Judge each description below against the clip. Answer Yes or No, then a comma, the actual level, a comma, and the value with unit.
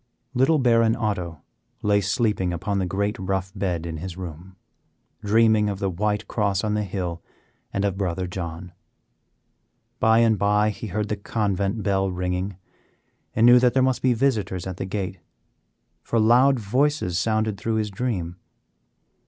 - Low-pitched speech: Yes, low, 100 Hz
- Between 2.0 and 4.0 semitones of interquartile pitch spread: Yes, average, 3.3 semitones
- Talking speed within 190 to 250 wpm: No, average, 160 wpm